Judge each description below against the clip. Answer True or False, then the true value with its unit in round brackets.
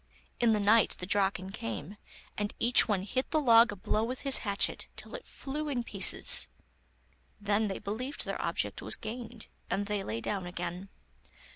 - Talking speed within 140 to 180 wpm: True (175 wpm)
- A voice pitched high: True (210 Hz)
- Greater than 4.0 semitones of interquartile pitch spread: False (3.6 semitones)